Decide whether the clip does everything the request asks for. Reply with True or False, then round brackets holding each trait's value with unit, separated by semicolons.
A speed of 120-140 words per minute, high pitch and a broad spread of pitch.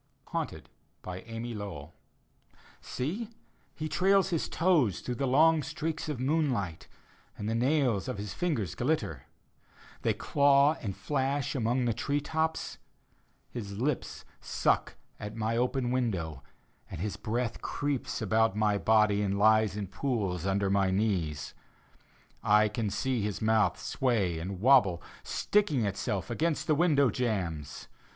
False (135 wpm; 115 Hz; 5.8 semitones)